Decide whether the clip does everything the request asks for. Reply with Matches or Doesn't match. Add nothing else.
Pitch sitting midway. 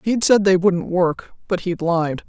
Matches